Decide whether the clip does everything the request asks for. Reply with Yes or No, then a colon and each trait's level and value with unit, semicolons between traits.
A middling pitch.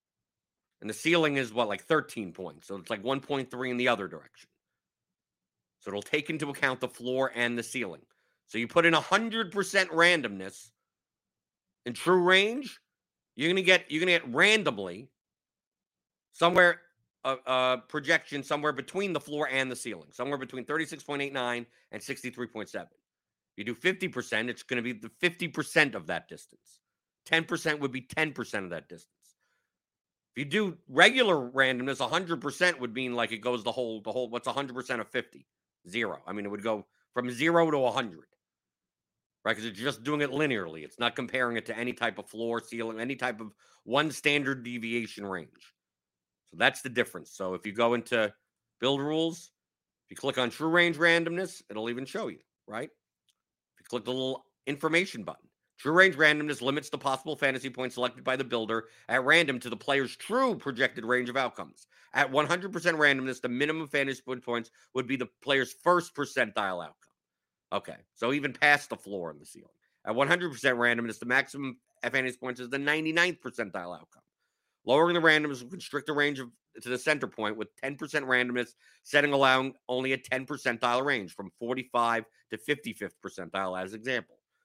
No: low, 130 Hz